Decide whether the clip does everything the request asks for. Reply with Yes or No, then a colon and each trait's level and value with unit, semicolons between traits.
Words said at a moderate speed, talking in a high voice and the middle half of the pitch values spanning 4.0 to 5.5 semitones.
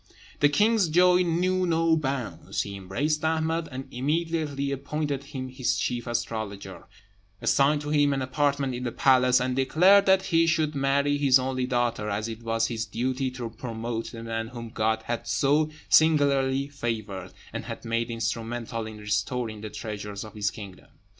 No: average, 165 wpm; low, 130 Hz; average, 4.5 semitones